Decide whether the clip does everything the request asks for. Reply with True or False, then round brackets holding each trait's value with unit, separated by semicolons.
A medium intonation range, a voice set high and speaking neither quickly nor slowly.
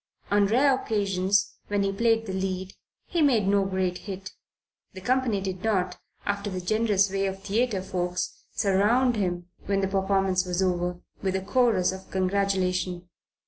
False (1.7 semitones; 195 Hz; 165 wpm)